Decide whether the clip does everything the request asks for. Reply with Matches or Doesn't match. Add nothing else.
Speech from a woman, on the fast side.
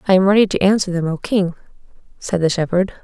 Matches